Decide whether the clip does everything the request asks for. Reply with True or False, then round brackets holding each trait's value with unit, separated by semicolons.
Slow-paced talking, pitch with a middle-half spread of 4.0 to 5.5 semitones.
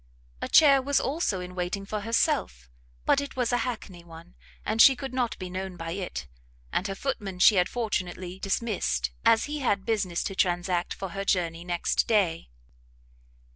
False (175 wpm; 4.6 semitones)